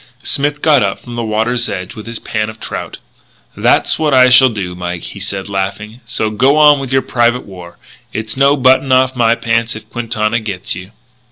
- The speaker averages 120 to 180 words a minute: No, average, 200 wpm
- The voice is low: Yes, low, 115 Hz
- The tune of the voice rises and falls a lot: No, average, 3.9 semitones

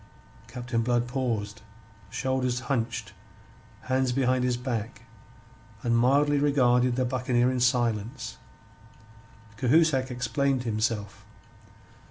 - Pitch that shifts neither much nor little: No, narrow, 1.8 semitones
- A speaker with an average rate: No, slow, 95 wpm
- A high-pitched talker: No, low, 125 Hz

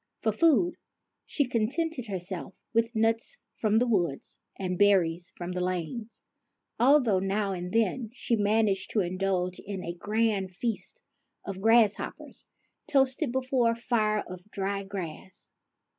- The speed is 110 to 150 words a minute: Yes, slow, 135 wpm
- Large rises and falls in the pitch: No, average, 3.9 semitones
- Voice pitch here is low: No, high, 210 Hz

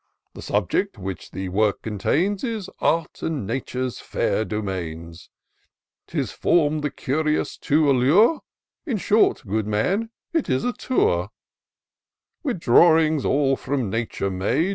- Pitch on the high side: No, low, 135 Hz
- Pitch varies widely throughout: Yes, wide, 8.3 semitones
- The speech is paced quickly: No, slow, 135 wpm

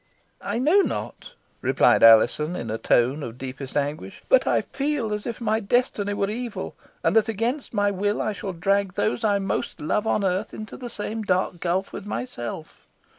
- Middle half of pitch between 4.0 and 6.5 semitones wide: Yes, average, 4.7 semitones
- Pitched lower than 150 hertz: No, high, 205 Hz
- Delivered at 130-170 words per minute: No, average, 185 wpm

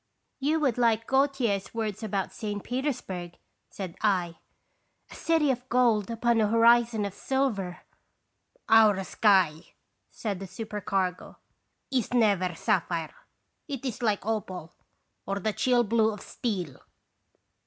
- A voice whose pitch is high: Yes, high, 215 Hz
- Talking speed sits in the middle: No, slow, 130 wpm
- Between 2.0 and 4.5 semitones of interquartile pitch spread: Yes, average, 3.9 semitones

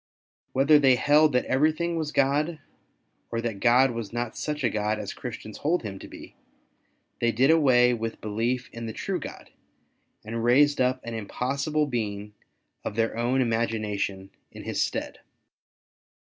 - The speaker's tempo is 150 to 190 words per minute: Yes, average, 160 wpm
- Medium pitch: No, low, 120 Hz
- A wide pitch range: No, average, 3.9 semitones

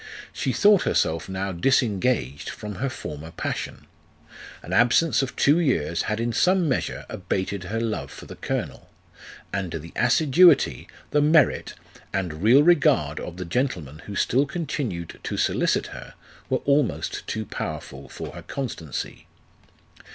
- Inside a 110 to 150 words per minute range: Yes, average, 145 wpm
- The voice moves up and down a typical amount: No, wide, 8.2 semitones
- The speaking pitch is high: No, low, 115 Hz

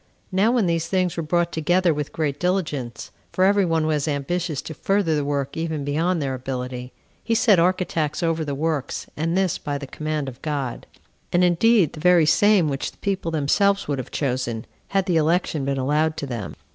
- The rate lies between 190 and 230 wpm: Yes, average, 195 wpm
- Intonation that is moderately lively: Yes, average, 4.1 semitones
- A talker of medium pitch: Yes, medium, 160 Hz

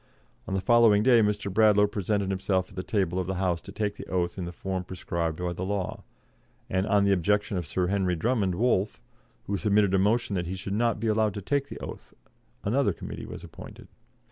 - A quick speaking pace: Yes, fast, 220 wpm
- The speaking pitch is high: No, low, 100 Hz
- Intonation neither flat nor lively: No, narrow, 2.3 semitones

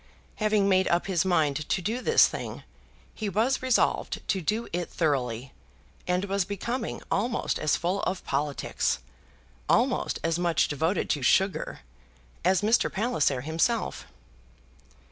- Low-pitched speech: No, medium, 185 Hz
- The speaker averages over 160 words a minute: No, slow, 135 wpm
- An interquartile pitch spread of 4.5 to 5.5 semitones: Yes, average, 4.9 semitones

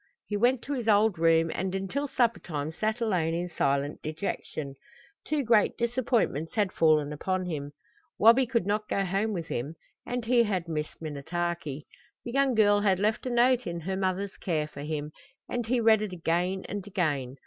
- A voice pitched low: No, high, 190 Hz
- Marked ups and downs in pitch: Yes, wide, 5.7 semitones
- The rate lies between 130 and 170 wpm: No, average, 180 wpm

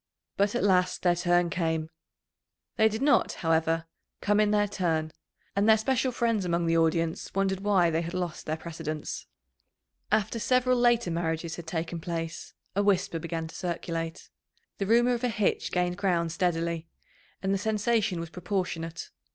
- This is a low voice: No, medium, 180 Hz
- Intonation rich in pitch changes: No, average, 3.9 semitones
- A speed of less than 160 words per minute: No, average, 165 wpm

